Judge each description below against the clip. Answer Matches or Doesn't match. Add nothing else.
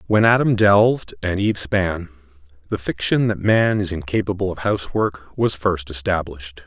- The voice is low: Matches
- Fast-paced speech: Doesn't match